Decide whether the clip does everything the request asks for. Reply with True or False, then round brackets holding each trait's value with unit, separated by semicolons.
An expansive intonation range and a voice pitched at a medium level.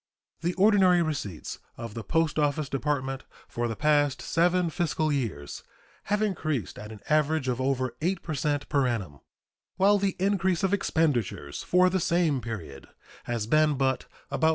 True (6.0 semitones; 150 Hz)